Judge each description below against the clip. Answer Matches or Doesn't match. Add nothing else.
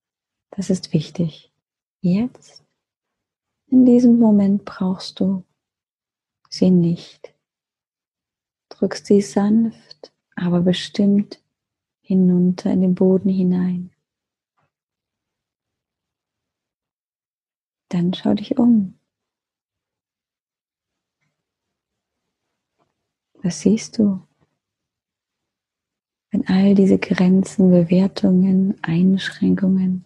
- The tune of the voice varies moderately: Doesn't match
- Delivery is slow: Matches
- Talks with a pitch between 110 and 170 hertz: Doesn't match